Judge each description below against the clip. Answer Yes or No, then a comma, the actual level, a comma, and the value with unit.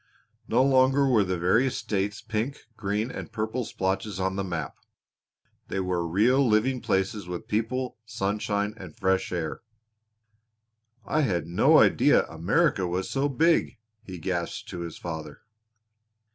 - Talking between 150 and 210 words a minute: No, average, 140 wpm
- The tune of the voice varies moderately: Yes, average, 4.9 semitones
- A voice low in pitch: Yes, low, 100 Hz